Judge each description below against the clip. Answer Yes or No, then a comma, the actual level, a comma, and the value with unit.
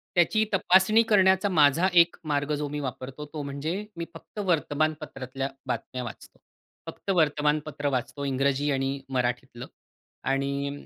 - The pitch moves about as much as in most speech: Yes, average, 3.5 semitones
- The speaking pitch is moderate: Yes, medium, 145 Hz